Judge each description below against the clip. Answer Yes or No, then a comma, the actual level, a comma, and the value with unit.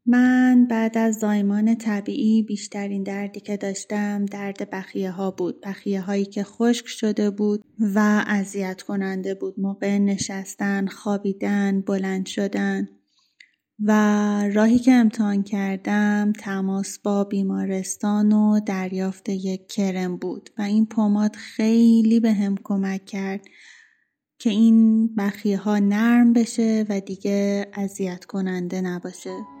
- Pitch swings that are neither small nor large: No, narrow, 1.7 semitones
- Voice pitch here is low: No, high, 205 Hz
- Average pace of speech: Yes, average, 120 wpm